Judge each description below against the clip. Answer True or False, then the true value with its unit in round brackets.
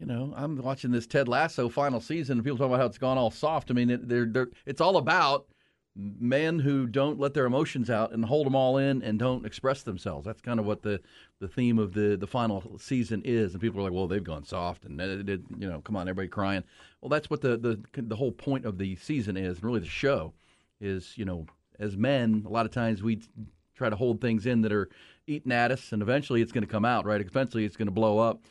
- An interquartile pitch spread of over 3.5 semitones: True (4.0 semitones)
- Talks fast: True (250 wpm)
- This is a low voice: True (115 Hz)